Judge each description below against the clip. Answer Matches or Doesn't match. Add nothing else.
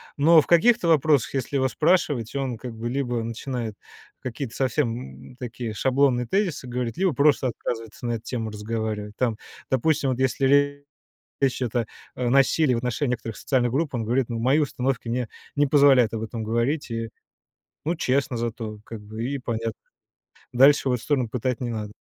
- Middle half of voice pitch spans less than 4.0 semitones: Matches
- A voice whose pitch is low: Matches